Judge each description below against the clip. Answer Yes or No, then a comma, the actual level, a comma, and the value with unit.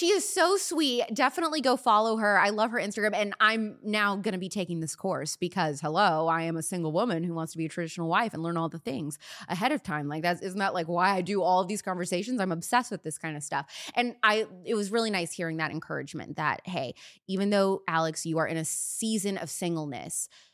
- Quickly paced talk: Yes, fast, 240 wpm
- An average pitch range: Yes, average, 4.8 semitones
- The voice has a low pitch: No, high, 190 Hz